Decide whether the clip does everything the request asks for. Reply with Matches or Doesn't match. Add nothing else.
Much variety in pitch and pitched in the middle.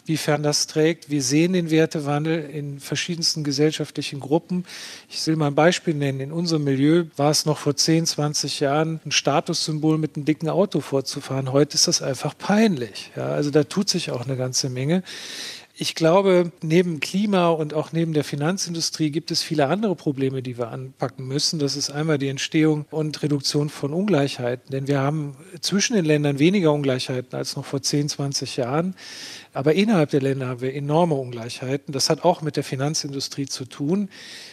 Doesn't match